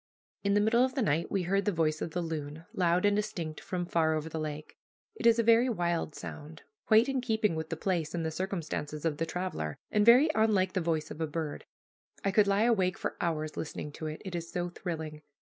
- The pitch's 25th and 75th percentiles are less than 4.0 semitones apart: No, average, 4.6 semitones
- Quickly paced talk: Yes, fast, 230 wpm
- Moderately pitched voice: Yes, medium, 175 Hz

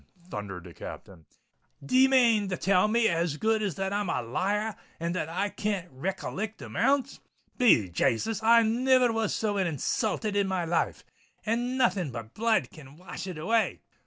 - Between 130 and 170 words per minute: Yes, average, 160 wpm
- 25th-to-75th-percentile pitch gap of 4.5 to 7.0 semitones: Yes, average, 5.3 semitones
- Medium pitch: No, high, 200 Hz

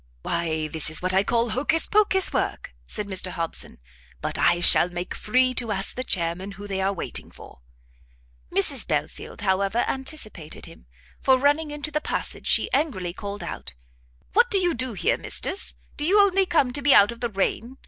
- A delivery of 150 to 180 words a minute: No, average, 190 wpm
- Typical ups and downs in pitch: No, wide, 7.7 semitones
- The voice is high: Yes, high, 230 Hz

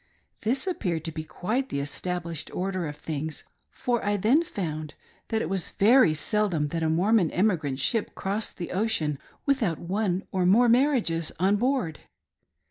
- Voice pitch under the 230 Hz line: Yes, medium, 185 Hz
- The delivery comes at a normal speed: Yes, average, 160 wpm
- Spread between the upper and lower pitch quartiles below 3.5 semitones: No, wide, 5.6 semitones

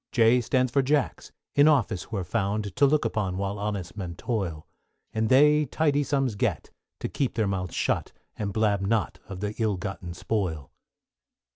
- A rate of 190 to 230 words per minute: No, average, 175 wpm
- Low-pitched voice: Yes, low, 105 Hz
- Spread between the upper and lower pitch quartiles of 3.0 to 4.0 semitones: No, average, 4.9 semitones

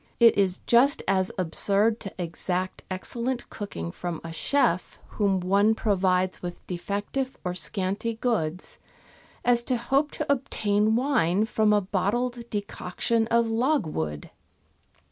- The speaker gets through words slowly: Yes, slow, 125 wpm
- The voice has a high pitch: Yes, high, 205 Hz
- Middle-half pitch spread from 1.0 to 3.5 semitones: No, average, 4.3 semitones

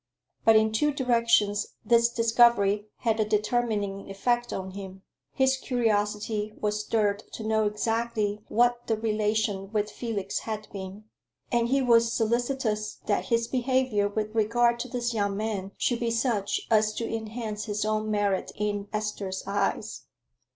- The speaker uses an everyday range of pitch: No, narrow, 2.2 semitones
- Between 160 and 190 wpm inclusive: No, average, 150 wpm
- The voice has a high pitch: Yes, high, 215 Hz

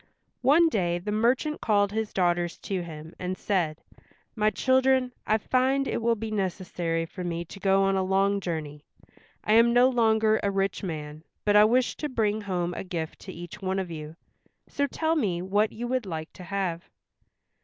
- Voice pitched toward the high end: Yes, high, 195 Hz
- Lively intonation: No, average, 4.5 semitones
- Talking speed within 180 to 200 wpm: Yes, average, 190 wpm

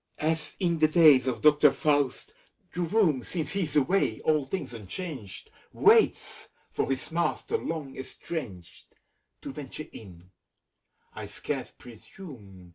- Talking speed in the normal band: No, slow, 125 wpm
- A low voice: No, medium, 150 Hz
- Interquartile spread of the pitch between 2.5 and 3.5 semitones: No, average, 4.7 semitones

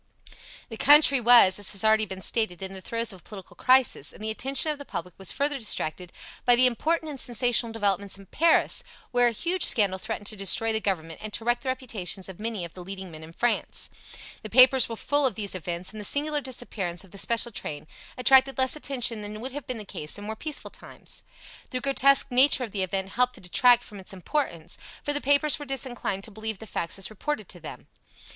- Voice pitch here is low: No, high, 225 Hz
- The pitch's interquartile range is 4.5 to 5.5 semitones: Yes, average, 5.1 semitones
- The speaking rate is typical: No, fast, 225 wpm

